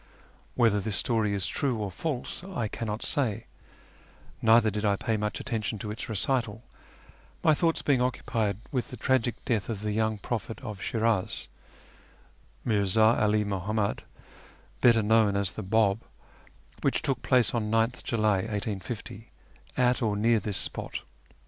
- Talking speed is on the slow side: No, average, 150 wpm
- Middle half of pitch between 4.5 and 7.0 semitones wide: No, narrow, 2.4 semitones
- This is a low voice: Yes, low, 110 Hz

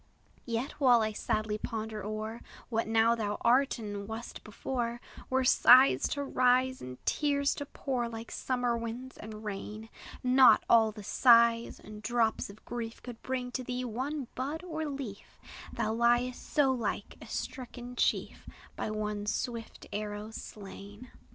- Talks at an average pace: Yes, average, 150 wpm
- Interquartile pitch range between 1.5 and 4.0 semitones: Yes, average, 2.8 semitones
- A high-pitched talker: Yes, high, 235 Hz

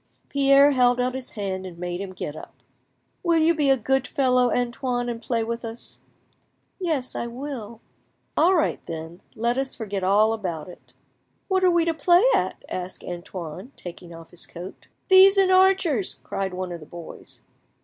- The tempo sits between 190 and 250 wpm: No, average, 180 wpm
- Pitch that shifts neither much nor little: No, wide, 7.2 semitones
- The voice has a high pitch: Yes, high, 240 Hz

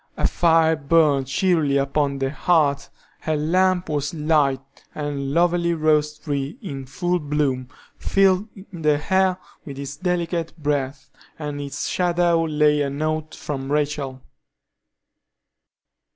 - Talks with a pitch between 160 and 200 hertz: No, medium, 150 Hz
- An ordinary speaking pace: No, slow, 125 wpm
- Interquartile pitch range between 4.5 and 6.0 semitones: No, average, 3.2 semitones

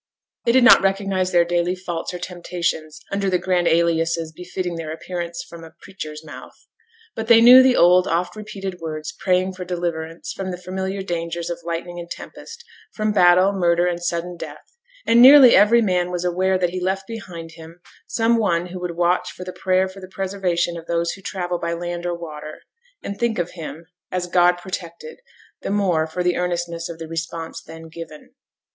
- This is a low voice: No, medium, 175 Hz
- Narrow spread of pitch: Yes, narrow, 2.0 semitones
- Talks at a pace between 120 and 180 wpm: No, average, 195 wpm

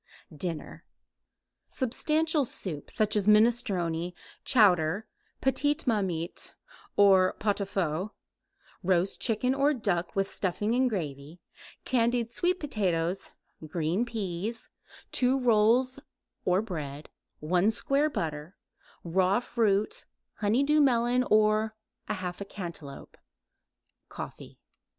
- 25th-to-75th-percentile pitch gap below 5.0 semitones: No, average, 5.3 semitones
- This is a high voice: Yes, high, 205 Hz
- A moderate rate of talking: No, slow, 100 wpm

